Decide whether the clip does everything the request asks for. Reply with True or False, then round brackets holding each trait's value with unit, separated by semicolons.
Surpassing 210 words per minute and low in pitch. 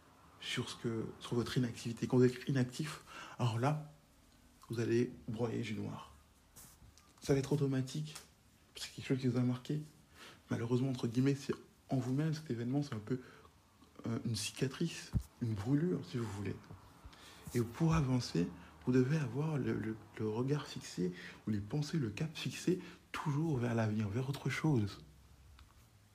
False (165 wpm; 125 Hz)